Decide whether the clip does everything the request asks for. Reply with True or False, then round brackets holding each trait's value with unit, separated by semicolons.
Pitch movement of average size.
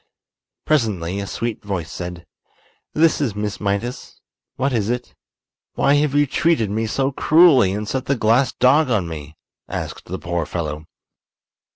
False (6.1 semitones)